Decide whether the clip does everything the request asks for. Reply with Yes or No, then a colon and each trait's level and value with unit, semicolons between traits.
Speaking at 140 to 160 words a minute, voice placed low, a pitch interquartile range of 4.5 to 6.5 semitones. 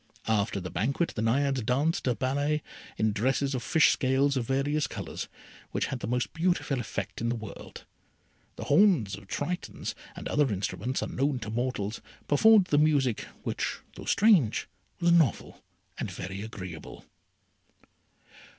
Yes: average, 150 wpm; low, 130 Hz; average, 5.1 semitones